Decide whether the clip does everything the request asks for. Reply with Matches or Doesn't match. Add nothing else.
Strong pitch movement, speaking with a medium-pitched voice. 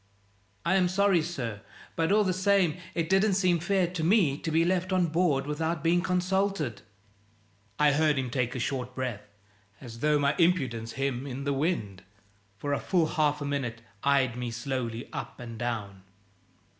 Matches